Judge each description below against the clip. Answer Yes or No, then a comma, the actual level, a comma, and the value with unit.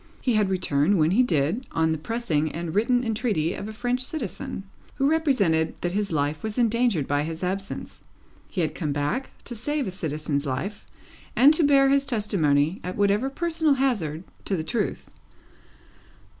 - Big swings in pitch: Yes, wide, 7.8 semitones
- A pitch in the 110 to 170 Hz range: No, high, 200 Hz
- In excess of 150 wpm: Yes, average, 170 wpm